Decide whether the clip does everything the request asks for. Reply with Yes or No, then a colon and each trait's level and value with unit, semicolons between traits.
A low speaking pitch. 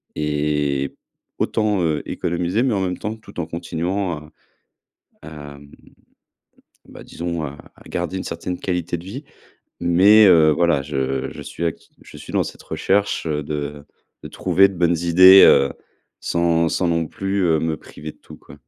Yes: very low, 85 Hz